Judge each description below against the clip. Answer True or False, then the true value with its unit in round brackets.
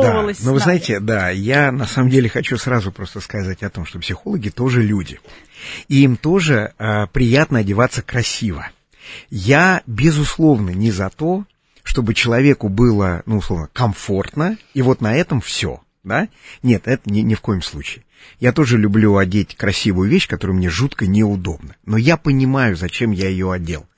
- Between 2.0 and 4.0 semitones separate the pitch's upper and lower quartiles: False (5.1 semitones)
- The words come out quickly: True (170 wpm)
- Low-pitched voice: True (110 Hz)